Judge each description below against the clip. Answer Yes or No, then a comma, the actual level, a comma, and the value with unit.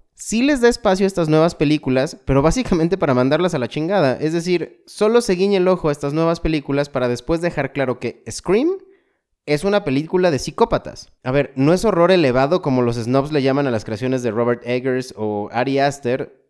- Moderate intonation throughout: No, wide, 5.8 semitones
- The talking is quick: Yes, fast, 205 wpm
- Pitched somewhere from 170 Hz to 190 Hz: No, medium, 150 Hz